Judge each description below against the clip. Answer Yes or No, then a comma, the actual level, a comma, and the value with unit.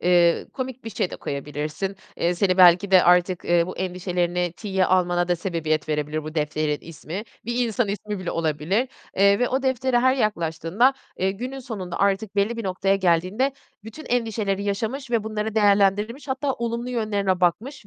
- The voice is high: Yes, high, 195 Hz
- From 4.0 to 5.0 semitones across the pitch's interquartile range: Yes, average, 4.6 semitones